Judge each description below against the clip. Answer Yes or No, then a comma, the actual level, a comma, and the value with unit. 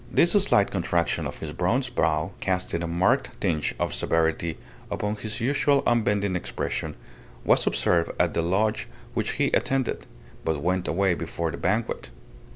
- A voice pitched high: No, very low, 95 Hz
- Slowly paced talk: No, average, 155 wpm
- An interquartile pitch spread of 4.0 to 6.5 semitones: Yes, average, 4.8 semitones